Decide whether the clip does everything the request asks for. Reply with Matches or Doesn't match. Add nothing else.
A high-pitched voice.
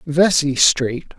Doesn't match